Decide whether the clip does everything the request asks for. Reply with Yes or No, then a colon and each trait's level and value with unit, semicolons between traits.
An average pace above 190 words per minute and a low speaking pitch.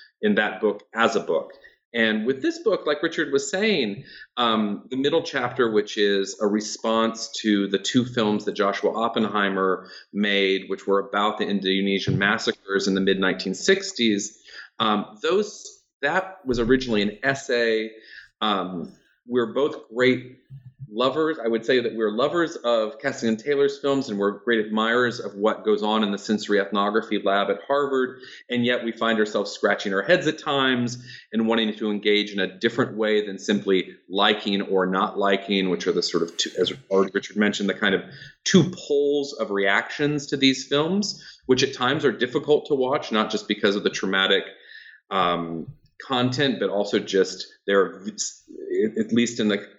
No: average, 175 wpm; low, 115 Hz